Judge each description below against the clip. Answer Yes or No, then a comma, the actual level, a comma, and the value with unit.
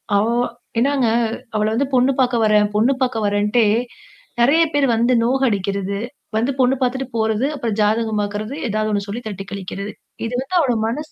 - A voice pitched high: Yes, high, 225 Hz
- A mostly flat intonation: No, average, 3.7 semitones